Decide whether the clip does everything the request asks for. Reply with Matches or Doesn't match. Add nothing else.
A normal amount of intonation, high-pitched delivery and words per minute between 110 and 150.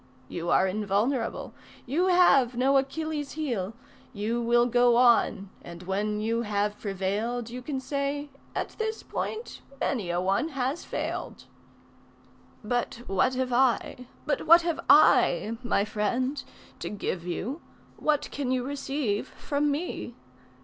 Matches